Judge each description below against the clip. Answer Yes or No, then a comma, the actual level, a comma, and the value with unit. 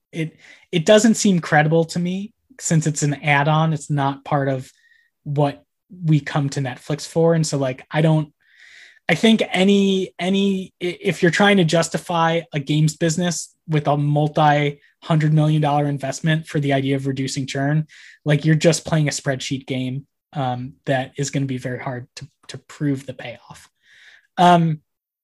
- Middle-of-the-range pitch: Yes, medium, 150 Hz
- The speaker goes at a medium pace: Yes, average, 180 wpm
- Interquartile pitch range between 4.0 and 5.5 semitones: No, average, 3.5 semitones